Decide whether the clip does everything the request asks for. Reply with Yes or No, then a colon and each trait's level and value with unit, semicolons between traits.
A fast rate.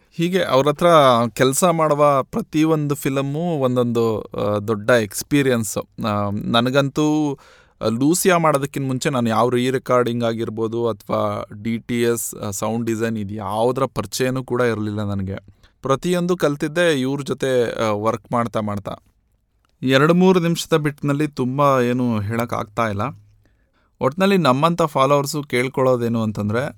Yes: fast, 115 wpm